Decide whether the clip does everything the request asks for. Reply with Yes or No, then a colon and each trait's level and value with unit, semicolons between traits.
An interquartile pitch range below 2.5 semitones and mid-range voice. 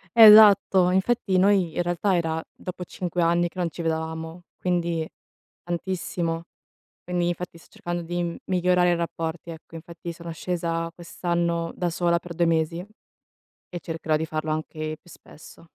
Yes: narrow, 1.5 semitones; medium, 170 Hz